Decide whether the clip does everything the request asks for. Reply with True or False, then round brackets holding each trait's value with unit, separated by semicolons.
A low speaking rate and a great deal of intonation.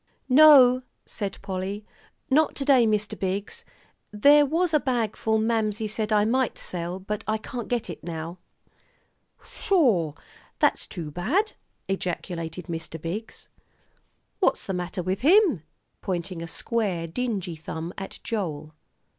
True (130 wpm; 5.8 semitones)